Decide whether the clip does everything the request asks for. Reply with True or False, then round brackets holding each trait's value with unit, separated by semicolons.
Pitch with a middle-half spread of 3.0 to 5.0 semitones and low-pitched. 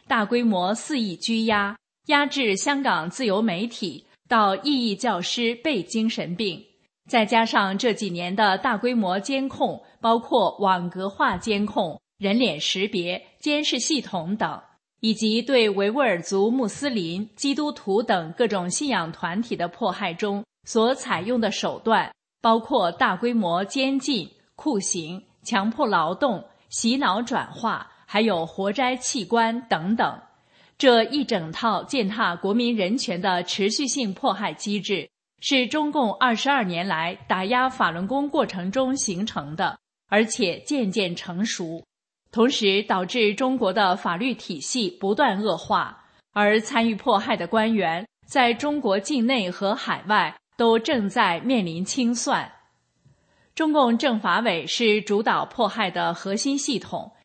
False (4.4 semitones; 220 Hz)